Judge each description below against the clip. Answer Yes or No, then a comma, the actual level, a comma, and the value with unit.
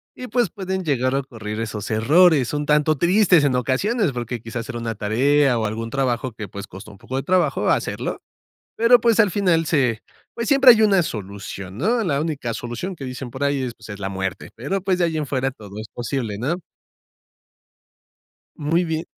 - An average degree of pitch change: No, wide, 7.5 semitones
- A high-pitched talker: No, low, 135 Hz